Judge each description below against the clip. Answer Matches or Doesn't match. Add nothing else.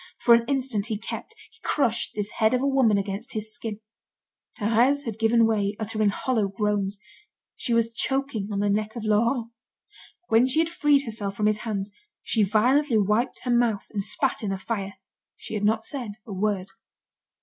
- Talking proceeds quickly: Doesn't match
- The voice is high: Matches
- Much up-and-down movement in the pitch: Doesn't match